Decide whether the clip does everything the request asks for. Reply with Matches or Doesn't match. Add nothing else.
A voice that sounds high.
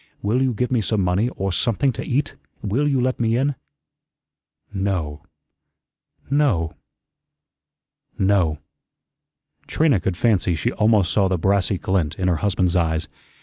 Doesn't match